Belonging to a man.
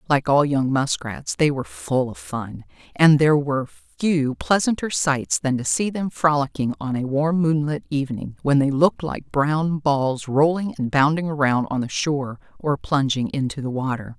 No: female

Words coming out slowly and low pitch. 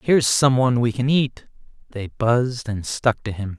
No: average, 200 wpm; low, 120 Hz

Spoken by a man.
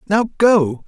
Yes: male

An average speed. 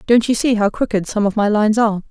No: fast, 285 wpm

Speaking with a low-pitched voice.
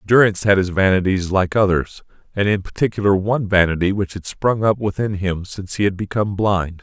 Yes: low, 100 Hz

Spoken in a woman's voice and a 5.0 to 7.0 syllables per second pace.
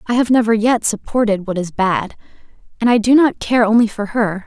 Yes: female; 5.4 syllables/s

